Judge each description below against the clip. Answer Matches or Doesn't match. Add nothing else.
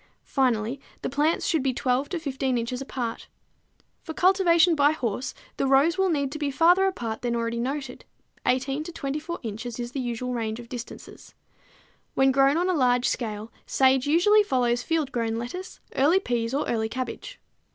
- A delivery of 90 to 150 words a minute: Doesn't match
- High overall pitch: Matches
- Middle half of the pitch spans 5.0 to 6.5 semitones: Doesn't match